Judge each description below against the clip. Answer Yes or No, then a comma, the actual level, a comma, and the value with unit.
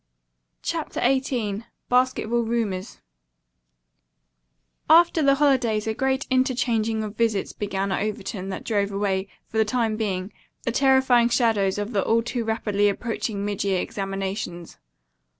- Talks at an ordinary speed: No, slow, 130 wpm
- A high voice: Yes, high, 220 Hz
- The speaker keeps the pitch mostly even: No, average, 3.5 semitones